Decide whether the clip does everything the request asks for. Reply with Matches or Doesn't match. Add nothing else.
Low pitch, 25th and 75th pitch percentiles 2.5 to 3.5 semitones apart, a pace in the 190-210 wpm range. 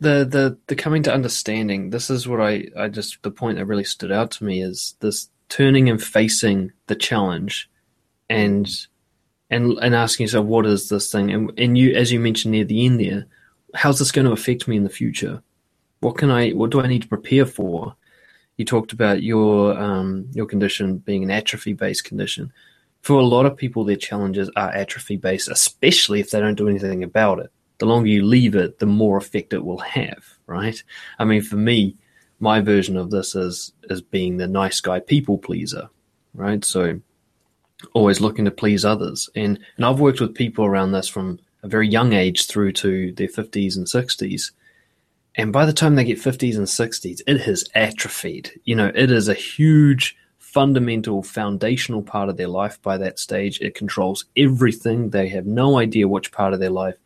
Matches